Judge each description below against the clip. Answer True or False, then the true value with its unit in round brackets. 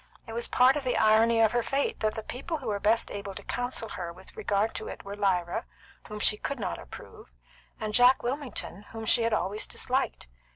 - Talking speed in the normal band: False (220 wpm)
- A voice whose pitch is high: True (220 Hz)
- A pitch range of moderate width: True (3.3 semitones)